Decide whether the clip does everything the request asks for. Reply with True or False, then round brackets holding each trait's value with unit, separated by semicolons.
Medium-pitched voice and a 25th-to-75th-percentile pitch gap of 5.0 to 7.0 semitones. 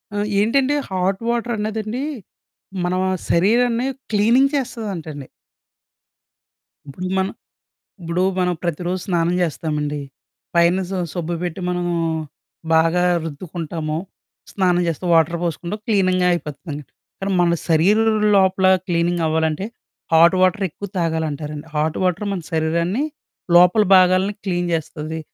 False (175 Hz; 3.4 semitones)